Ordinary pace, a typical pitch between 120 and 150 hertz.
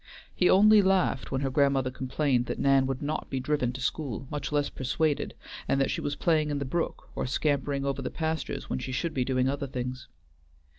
No: fast, 210 wpm; medium, 140 Hz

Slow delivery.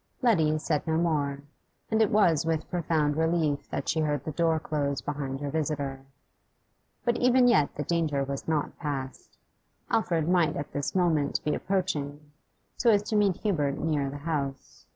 No: average, 170 wpm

